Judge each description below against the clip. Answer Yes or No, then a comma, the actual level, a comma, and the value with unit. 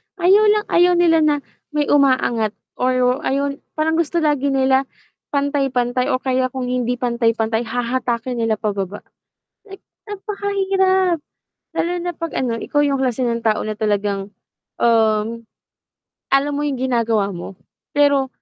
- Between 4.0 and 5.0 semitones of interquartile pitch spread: Yes, average, 4.5 semitones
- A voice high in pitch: Yes, very high, 260 Hz